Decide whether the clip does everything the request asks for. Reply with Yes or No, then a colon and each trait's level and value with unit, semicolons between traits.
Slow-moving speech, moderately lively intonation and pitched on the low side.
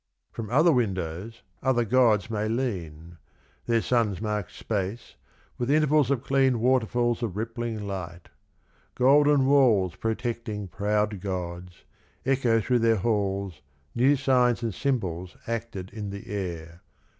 Yes: slow, 125 wpm; average, 4.2 semitones; low, 110 Hz